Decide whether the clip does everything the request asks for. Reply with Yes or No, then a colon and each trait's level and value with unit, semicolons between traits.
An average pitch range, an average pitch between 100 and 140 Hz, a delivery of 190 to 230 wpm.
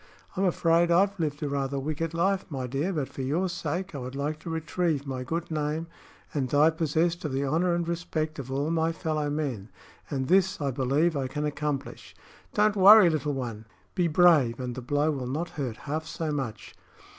No: average, 3.6 semitones; medium, 150 Hz; average, 200 wpm